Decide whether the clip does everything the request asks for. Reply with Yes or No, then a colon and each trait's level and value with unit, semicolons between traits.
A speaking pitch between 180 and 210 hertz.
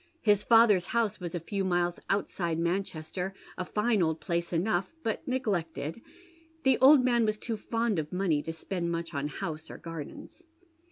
Yes: medium, 185 Hz